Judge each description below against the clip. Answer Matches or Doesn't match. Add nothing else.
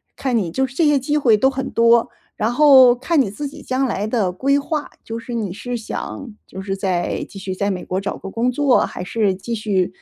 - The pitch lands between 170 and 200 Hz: Doesn't match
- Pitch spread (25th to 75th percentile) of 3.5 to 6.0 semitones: Matches